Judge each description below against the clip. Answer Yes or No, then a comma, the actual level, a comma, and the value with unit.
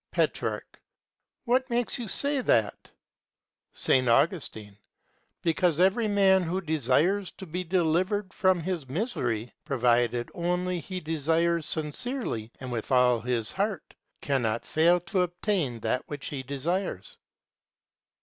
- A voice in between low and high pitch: Yes, medium, 165 Hz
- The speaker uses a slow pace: Yes, slow, 120 wpm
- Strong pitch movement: Yes, wide, 6.8 semitones